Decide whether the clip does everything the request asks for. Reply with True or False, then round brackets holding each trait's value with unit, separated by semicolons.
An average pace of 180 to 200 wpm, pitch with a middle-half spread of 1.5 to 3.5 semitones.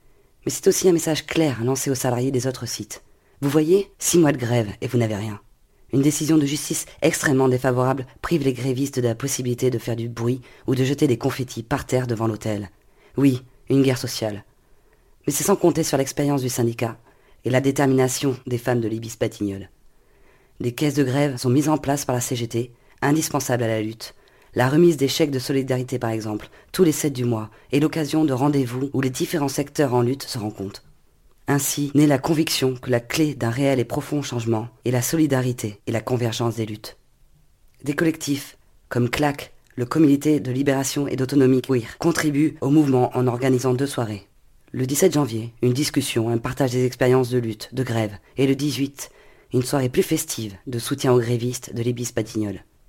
True (195 wpm; 3.2 semitones)